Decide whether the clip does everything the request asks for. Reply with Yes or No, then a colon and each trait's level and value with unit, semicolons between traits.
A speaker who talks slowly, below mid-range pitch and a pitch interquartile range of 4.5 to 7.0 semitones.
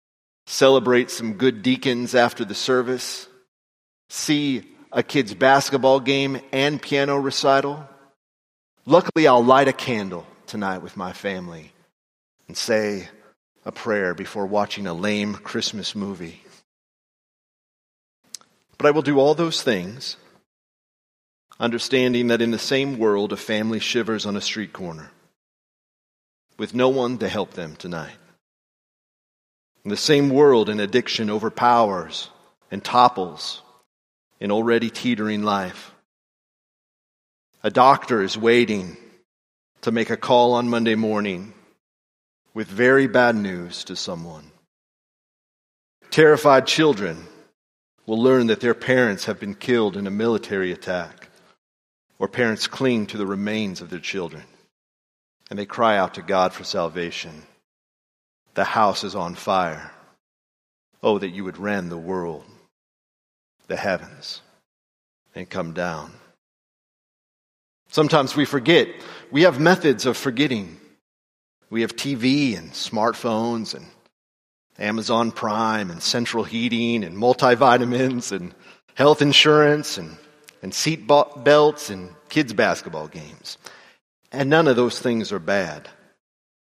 Yes: slow, 125 wpm; low, 115 Hz; average, 5.1 semitones